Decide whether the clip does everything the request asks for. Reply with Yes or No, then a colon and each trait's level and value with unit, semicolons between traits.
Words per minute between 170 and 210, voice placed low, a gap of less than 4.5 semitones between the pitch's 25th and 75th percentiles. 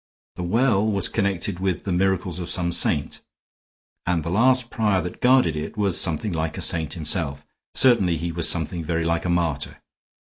Yes: average, 180 wpm; very low, 90 Hz; average, 3.2 semitones